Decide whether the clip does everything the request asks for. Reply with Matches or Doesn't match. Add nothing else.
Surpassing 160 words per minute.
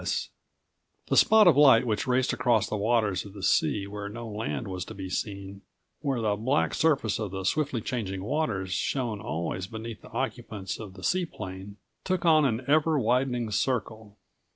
Matches